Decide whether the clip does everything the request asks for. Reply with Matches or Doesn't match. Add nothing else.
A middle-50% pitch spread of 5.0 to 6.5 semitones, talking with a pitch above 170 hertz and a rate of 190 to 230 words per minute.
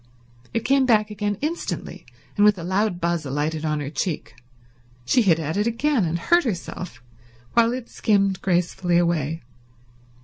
Doesn't match